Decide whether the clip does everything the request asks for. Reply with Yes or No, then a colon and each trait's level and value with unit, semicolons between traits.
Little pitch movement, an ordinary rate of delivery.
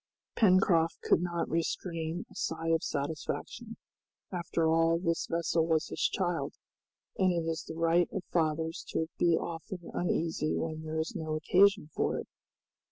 Yes: narrow, 1.4 semitones; average, 155 wpm